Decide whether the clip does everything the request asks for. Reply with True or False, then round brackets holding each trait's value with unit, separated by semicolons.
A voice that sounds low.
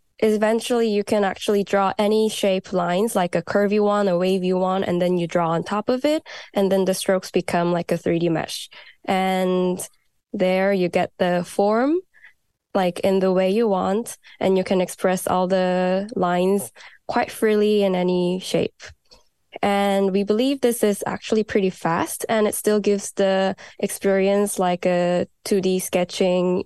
False (190 Hz)